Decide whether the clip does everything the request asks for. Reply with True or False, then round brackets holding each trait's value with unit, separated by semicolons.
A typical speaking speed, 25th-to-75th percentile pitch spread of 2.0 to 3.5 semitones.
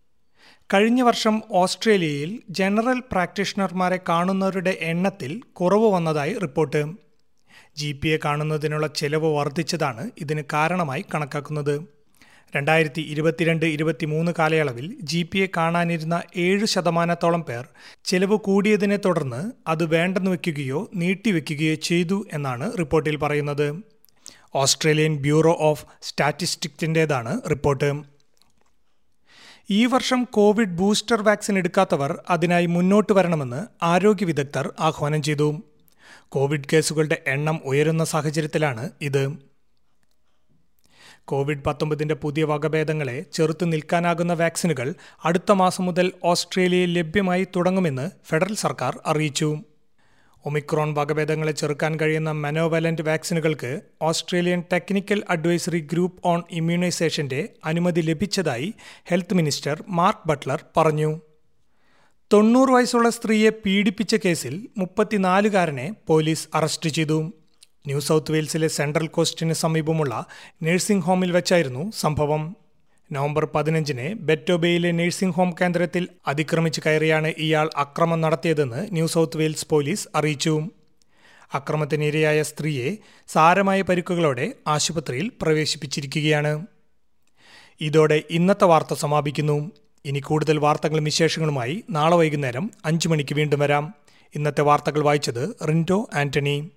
True (100 wpm; 3.2 semitones)